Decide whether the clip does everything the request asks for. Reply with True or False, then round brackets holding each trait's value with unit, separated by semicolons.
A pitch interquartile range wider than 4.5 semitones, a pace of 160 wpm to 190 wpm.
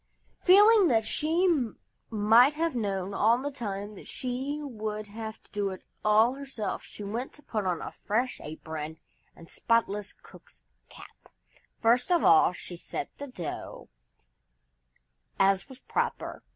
False (5.0 semitones; 145 wpm)